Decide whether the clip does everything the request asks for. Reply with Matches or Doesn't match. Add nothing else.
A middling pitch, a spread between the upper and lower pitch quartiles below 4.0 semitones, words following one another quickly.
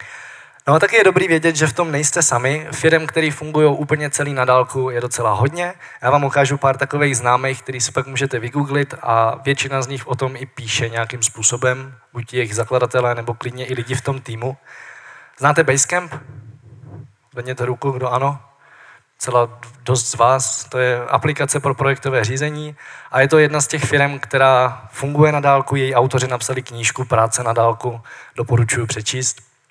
Doesn't match